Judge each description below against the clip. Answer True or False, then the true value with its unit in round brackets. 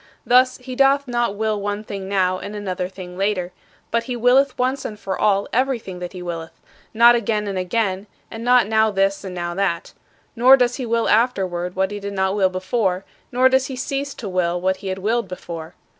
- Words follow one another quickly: True (210 wpm)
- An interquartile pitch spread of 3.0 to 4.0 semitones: False (4.4 semitones)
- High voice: True (205 Hz)